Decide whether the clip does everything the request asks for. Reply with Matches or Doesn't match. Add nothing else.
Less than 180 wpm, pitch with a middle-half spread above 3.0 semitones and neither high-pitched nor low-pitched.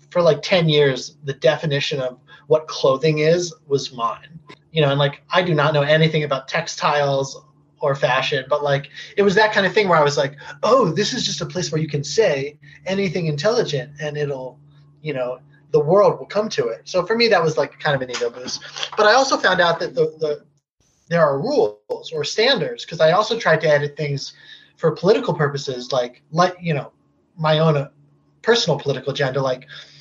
Doesn't match